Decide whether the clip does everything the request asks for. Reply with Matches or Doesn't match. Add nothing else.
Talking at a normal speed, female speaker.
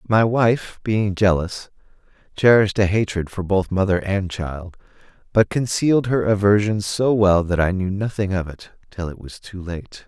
Doesn't match